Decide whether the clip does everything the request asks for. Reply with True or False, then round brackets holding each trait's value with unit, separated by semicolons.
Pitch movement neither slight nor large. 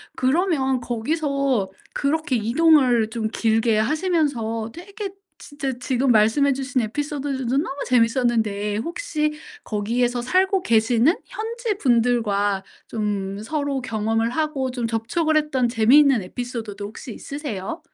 True (4.9 semitones)